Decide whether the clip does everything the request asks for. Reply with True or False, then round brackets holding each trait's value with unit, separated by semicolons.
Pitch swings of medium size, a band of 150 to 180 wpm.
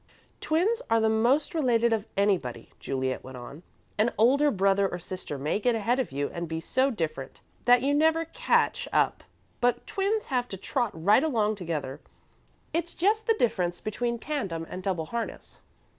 False (8.1 semitones; 175 wpm)